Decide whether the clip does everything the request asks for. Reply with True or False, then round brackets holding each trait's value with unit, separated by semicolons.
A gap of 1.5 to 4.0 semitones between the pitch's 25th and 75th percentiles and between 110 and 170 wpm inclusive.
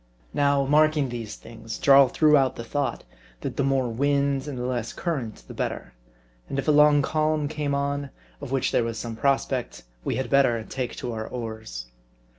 False (3.3 semitones; 190 wpm)